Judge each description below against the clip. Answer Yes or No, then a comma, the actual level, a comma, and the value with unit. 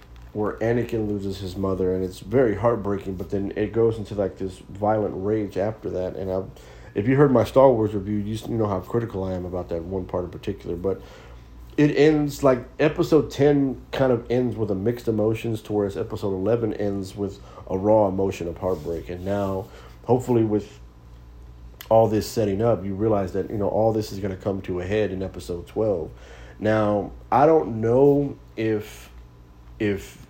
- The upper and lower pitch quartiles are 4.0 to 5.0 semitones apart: No, average, 3.2 semitones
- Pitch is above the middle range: No, low, 105 Hz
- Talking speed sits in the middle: Yes, average, 190 wpm